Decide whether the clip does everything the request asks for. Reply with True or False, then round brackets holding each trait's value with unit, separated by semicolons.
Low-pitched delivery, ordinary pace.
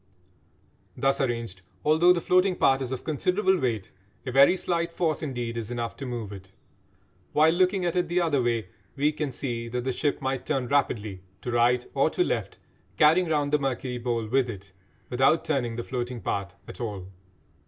True (130 Hz; 185 wpm)